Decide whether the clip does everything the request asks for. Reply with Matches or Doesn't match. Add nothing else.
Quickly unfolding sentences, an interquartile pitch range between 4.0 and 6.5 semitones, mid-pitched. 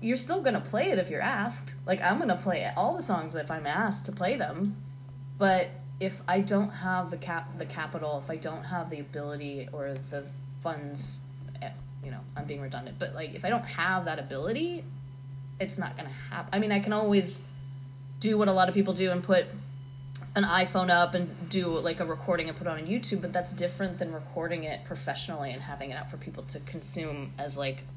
Matches